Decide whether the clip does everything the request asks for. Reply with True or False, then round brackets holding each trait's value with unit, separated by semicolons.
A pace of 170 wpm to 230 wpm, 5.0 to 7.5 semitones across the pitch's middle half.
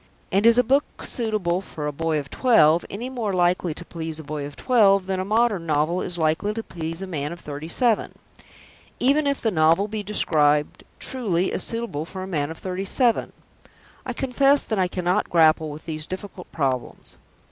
True (195 wpm; 5.6 semitones)